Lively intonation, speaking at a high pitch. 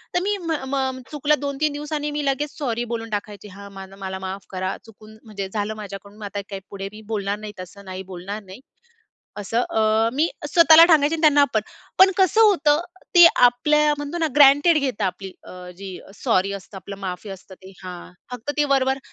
Yes: wide, 6.8 semitones; high, 225 Hz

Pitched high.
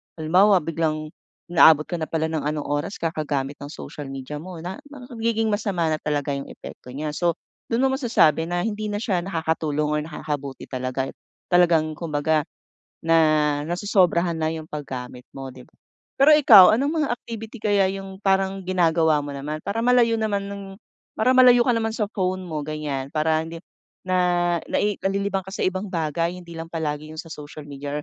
No: medium, 170 Hz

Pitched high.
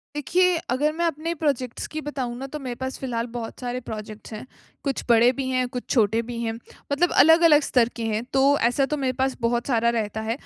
Yes: very high, 255 Hz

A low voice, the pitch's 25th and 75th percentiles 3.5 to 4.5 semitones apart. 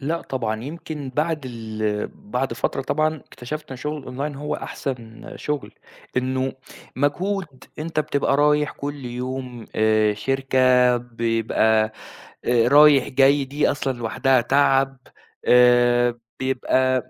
No: low, 130 Hz; average, 3.0 semitones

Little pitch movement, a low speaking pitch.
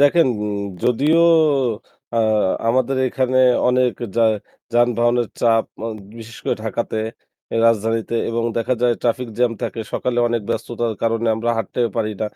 Yes: narrow, 1.6 semitones; low, 120 Hz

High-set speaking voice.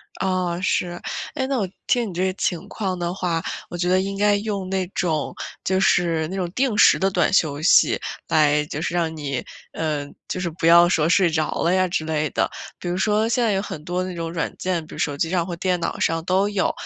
No: medium, 180 Hz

